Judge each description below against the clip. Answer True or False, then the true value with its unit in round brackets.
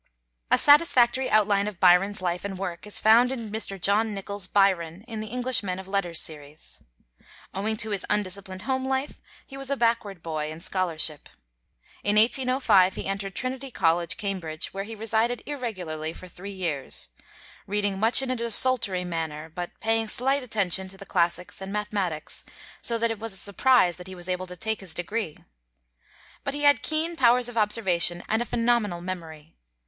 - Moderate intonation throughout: True (4.5 semitones)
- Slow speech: False (180 wpm)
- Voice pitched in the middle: False (200 Hz)